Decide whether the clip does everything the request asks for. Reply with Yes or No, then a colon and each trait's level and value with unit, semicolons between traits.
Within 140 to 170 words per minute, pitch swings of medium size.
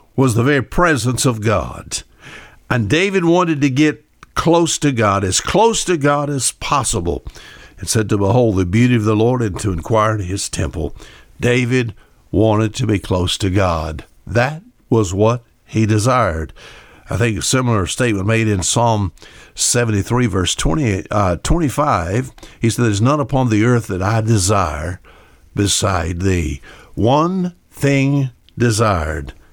Yes: average, 155 wpm; average, 4.7 semitones